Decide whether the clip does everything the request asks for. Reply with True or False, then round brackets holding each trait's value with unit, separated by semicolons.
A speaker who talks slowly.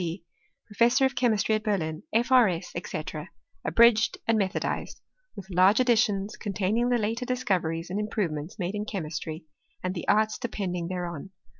False (170 wpm)